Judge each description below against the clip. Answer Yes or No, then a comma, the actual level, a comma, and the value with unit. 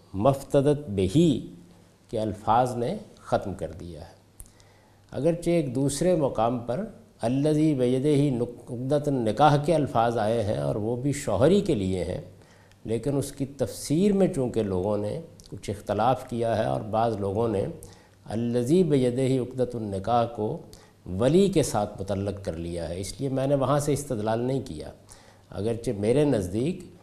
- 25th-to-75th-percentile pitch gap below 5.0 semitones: No, average, 5.3 semitones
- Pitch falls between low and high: No, low, 120 Hz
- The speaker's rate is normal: Yes, average, 155 wpm